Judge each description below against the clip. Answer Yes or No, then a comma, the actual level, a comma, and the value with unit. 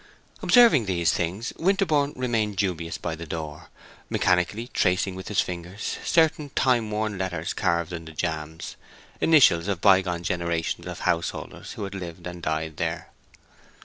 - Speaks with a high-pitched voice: No, very low, 90 Hz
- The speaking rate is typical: Yes, average, 145 wpm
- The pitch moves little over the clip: No, average, 4.3 semitones